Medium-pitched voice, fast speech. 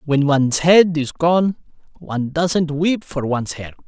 No: medium, 155 Hz; average, 170 wpm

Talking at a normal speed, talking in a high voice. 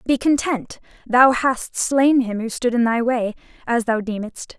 Yes: average, 185 wpm; high, 245 Hz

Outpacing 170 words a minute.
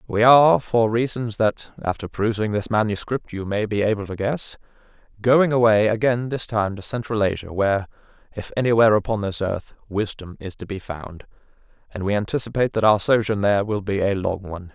Yes: average, 185 wpm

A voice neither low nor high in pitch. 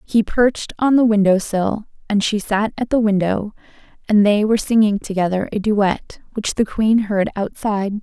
No: high, 210 Hz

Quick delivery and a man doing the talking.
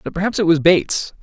Yes: fast, 245 wpm; male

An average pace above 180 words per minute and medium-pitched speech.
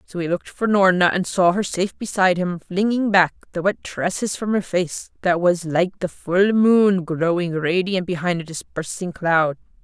Yes: average, 190 wpm; medium, 180 Hz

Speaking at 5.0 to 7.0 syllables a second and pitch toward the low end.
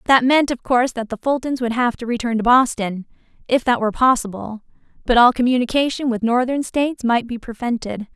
No: 5.8 syllables/s; high, 240 Hz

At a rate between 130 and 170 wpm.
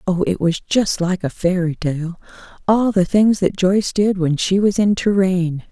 No: average, 200 wpm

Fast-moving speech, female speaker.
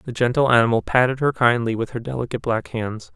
No: fast, 210 wpm; male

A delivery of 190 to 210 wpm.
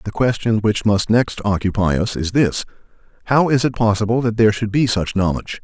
Yes: average, 200 wpm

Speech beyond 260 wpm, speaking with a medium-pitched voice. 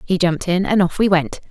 Yes: fast, 280 wpm; medium, 180 Hz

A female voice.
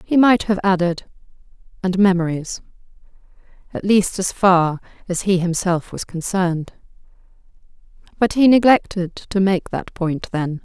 Yes: female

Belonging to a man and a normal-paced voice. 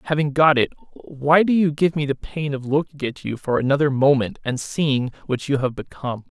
No: male; fast, 215 wpm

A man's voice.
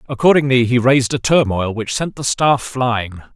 Yes: male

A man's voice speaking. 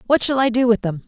No: female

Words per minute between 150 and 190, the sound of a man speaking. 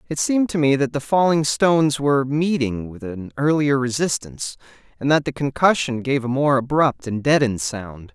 Yes: average, 185 wpm; male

